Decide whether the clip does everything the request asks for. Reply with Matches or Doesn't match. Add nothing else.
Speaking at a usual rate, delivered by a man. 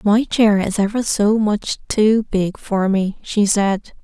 Doesn't match